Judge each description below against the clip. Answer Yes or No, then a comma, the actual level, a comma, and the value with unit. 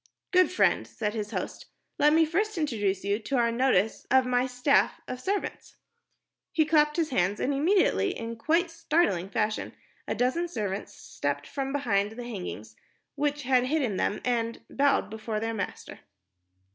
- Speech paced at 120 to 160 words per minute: Yes, average, 155 wpm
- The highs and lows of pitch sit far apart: Yes, wide, 6.1 semitones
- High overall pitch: Yes, very high, 250 Hz